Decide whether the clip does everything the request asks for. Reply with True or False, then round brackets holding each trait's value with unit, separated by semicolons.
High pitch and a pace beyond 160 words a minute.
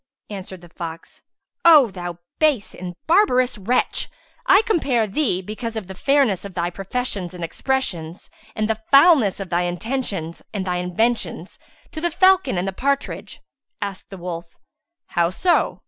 False (205 Hz; 155 wpm)